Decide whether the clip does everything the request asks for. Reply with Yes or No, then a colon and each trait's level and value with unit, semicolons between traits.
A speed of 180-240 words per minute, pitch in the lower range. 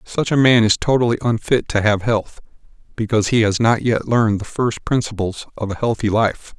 Yes: average, 200 wpm; low, 110 Hz